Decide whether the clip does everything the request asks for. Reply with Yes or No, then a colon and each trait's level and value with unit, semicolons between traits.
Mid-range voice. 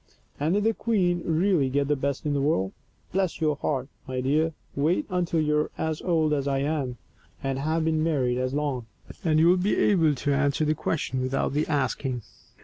Yes: medium, 150 Hz